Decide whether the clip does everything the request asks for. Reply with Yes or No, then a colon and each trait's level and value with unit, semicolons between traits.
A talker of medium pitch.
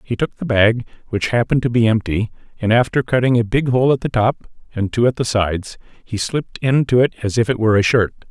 No: low, 115 Hz